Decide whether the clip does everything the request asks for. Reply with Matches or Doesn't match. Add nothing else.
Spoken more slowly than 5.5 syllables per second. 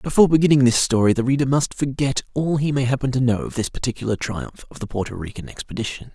Doesn't match